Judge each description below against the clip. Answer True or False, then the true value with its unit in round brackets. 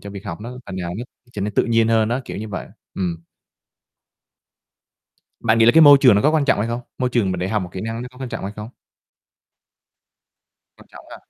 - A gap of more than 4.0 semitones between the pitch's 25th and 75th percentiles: False (3.5 semitones)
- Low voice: True (110 Hz)